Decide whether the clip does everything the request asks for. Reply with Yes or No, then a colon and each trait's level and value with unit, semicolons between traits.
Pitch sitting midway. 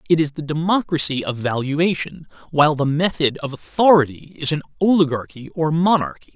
Yes: medium, 155 Hz